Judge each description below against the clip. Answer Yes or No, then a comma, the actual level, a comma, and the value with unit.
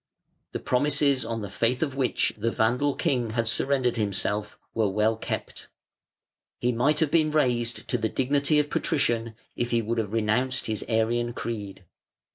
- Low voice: Yes, low, 120 Hz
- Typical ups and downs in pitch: Yes, average, 3.4 semitones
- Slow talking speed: No, average, 165 wpm